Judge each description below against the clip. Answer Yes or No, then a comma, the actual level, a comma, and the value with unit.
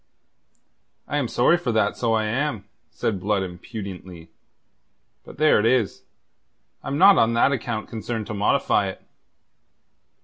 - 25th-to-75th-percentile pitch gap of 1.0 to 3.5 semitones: No, average, 3.9 semitones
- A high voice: No, low, 110 Hz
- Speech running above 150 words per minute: No, average, 140 wpm